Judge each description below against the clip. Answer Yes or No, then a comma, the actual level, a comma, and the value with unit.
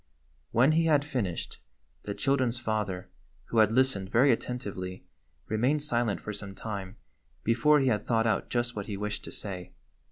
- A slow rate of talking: No, average, 165 wpm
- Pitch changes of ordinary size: Yes, average, 4.1 semitones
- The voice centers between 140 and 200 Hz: No, low, 115 Hz